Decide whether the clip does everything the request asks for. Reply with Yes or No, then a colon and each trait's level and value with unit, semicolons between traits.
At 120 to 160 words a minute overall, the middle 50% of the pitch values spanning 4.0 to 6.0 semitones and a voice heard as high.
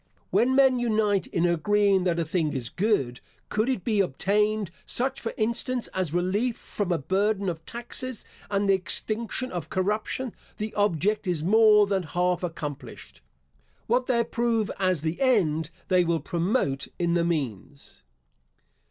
Yes: average, 150 wpm; average, 4.4 semitones; high, 195 Hz